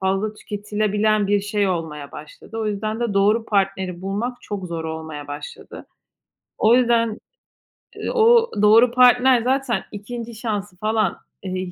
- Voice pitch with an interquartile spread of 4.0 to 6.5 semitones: No, average, 3.4 semitones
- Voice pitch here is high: Yes, high, 210 Hz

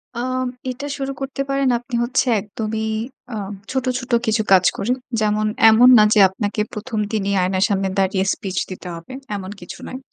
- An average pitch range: Yes, average, 4.2 semitones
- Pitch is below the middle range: No, high, 215 Hz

